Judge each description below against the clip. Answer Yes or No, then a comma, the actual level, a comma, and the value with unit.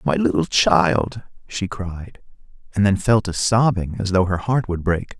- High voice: No, very low, 95 Hz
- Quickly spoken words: No, average, 185 wpm